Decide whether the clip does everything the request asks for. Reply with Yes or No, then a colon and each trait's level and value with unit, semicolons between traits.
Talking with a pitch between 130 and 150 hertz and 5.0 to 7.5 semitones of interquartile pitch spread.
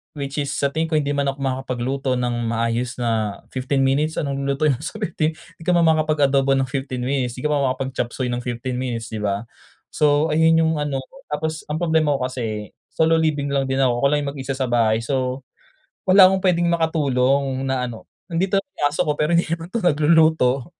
No: medium, 140 Hz; average, 3.7 semitones